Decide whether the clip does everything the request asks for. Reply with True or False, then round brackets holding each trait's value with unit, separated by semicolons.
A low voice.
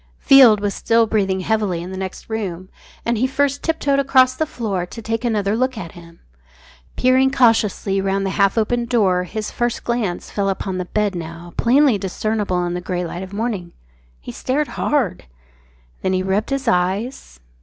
False (210 Hz)